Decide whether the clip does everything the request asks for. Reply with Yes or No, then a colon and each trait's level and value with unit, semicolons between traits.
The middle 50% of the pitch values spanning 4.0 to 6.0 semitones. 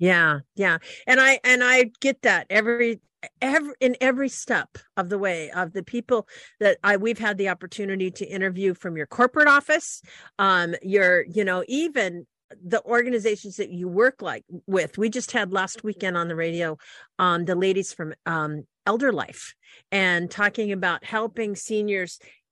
Yes: average, 4.7 semitones